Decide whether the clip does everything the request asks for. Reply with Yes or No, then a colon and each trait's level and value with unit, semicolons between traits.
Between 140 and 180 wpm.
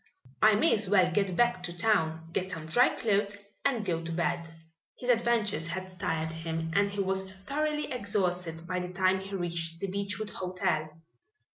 Yes: average, 175 wpm